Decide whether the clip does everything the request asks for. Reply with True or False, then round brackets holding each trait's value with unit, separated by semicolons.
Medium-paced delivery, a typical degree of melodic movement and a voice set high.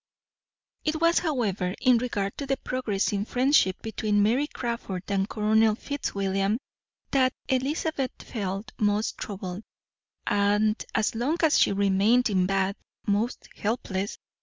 False (125 wpm; 4.2 semitones; 215 Hz)